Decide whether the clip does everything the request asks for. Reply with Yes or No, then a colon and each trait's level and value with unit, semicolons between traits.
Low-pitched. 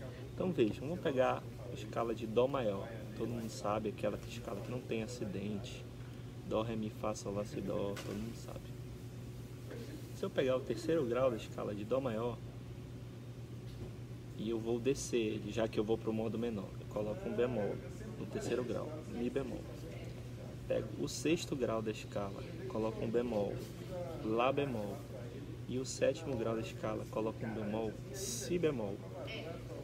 Yes: low, 120 Hz